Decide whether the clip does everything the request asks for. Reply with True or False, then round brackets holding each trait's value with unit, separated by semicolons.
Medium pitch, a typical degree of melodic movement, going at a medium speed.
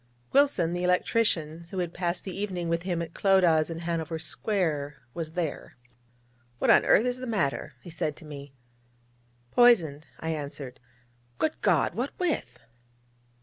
True (170 Hz; 3.5 semitones; 150 wpm)